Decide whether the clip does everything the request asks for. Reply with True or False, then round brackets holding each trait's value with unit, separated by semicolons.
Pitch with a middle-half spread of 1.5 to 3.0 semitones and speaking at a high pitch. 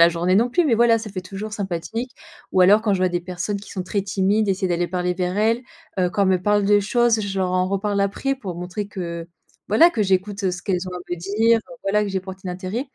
True (2.7 semitones; 195 Hz)